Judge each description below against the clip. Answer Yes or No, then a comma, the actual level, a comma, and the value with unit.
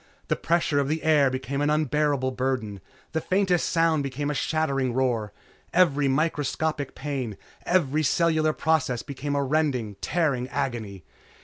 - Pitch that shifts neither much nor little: Yes, average, 3.2 semitones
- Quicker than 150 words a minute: No, average, 140 wpm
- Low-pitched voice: No, medium, 145 Hz